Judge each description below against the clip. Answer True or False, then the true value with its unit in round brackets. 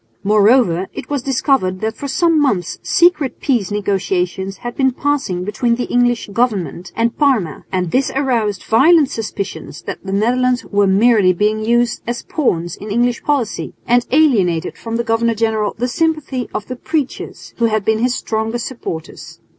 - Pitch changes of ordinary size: True (4.2 semitones)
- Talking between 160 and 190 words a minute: True (165 wpm)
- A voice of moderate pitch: False (230 Hz)